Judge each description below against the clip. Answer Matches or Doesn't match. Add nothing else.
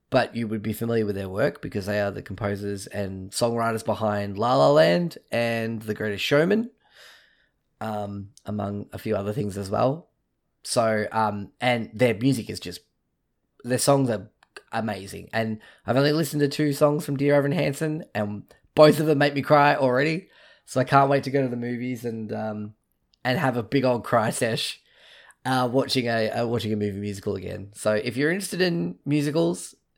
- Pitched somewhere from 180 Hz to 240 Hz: Doesn't match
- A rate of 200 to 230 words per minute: Doesn't match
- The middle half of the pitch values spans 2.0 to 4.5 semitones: Doesn't match